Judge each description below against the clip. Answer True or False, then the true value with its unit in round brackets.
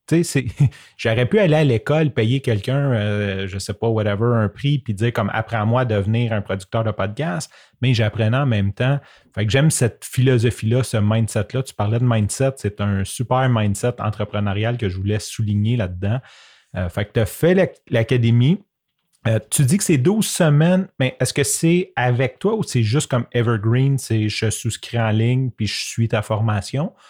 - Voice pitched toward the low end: True (120 Hz)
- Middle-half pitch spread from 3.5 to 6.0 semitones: True (4.1 semitones)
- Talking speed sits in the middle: True (200 wpm)